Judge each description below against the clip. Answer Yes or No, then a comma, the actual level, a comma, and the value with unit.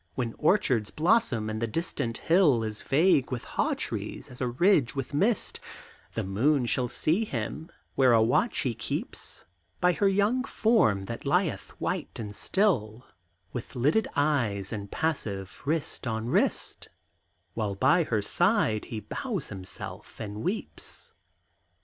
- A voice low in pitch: Yes, low, 130 Hz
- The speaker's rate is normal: Yes, average, 145 wpm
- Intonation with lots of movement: Yes, wide, 8.1 semitones